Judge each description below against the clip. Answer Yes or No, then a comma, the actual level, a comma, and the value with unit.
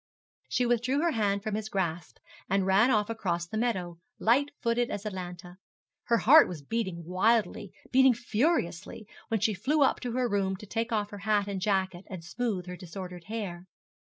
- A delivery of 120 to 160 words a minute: No, average, 185 wpm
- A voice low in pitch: No, high, 205 Hz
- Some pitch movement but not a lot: Yes, average, 4.0 semitones